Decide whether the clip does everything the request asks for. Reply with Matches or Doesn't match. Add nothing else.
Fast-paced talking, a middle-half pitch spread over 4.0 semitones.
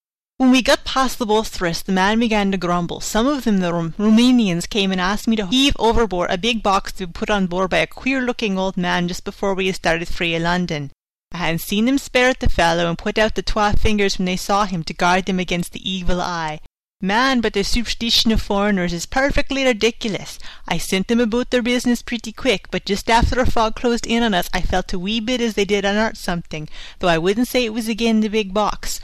Matches